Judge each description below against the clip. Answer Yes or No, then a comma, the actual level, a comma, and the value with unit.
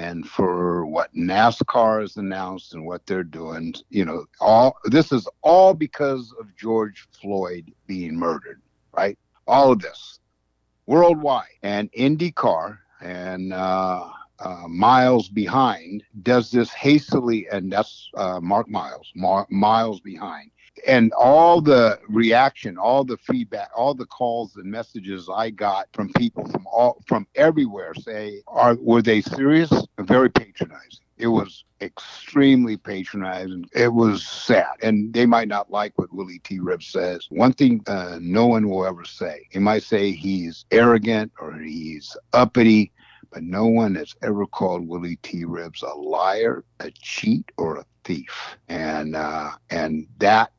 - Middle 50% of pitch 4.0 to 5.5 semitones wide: Yes, average, 4.5 semitones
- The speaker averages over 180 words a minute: No, average, 150 wpm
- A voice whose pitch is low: Yes, low, 105 Hz